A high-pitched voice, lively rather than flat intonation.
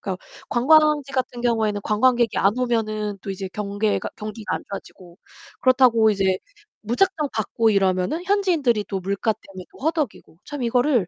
No: high, 225 Hz; average, 4.3 semitones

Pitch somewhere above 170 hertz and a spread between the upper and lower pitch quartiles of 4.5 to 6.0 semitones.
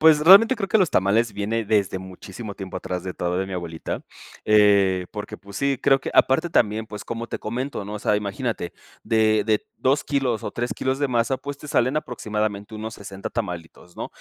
No: low, 110 Hz; average, 5.0 semitones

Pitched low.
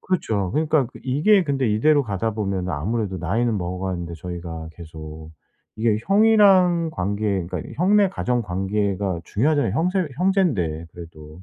Yes: low, 105 Hz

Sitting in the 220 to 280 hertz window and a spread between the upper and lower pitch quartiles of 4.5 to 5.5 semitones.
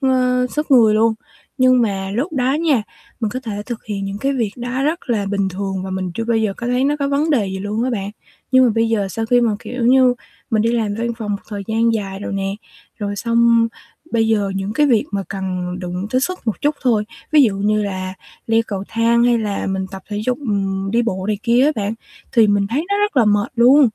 No: high, 225 Hz; average, 3.8 semitones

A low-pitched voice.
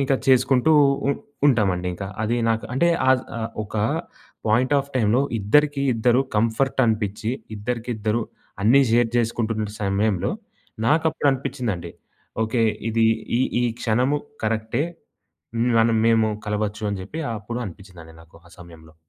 Yes: low, 115 Hz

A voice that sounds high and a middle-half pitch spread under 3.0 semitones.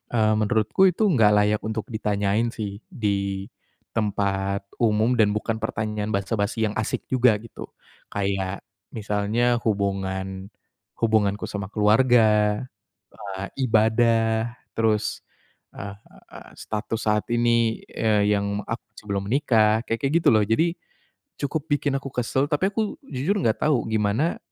No: low, 110 Hz; narrow, 2.5 semitones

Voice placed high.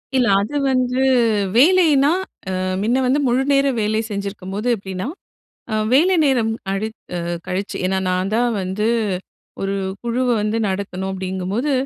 Yes: high, 220 Hz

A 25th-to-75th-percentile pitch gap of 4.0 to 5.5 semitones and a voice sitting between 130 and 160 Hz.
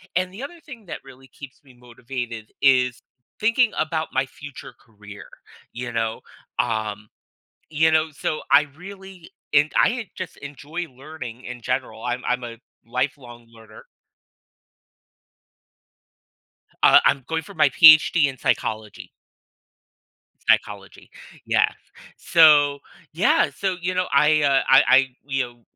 Yes: average, 4.7 semitones; medium, 140 Hz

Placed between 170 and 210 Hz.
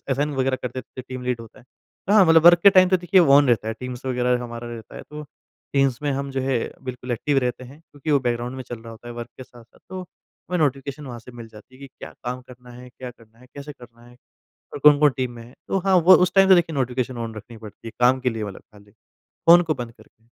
No: low, 130 Hz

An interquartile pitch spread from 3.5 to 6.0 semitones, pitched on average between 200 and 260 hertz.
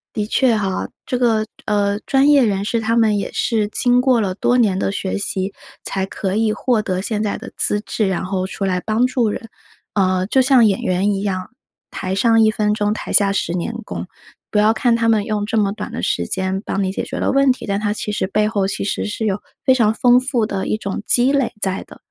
No: average, 2.8 semitones; high, 210 Hz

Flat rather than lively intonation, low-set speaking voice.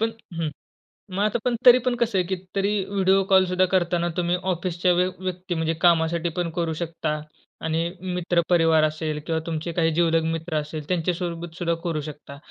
No: narrow, 2.3 semitones; medium, 170 Hz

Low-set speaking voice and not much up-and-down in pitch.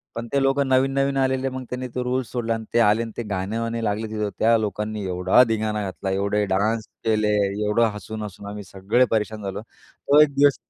No: low, 110 Hz; average, 3.4 semitones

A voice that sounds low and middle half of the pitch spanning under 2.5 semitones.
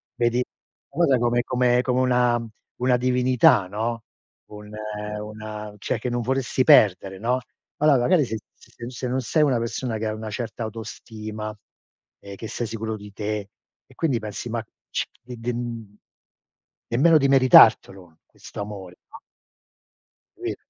No: low, 115 Hz; average, 2.8 semitones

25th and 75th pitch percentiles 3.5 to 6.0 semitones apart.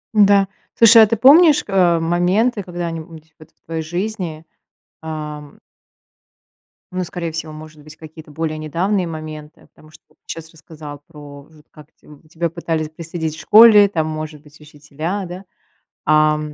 No: average, 2.7 semitones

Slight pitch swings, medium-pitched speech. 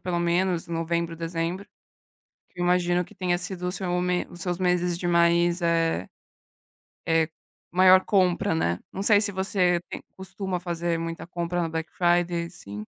Yes: narrow, 1.2 semitones; medium, 175 Hz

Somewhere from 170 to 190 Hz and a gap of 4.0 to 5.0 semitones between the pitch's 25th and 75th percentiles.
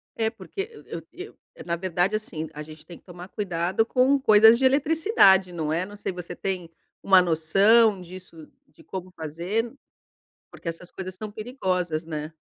Yes: medium, 185 Hz; average, 4.6 semitones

